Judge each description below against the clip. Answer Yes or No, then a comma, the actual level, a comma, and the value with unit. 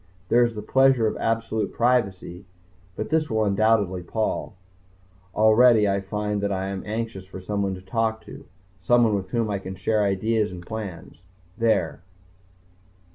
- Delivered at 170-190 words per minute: No, average, 155 wpm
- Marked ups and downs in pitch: No, average, 2.8 semitones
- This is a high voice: No, low, 105 Hz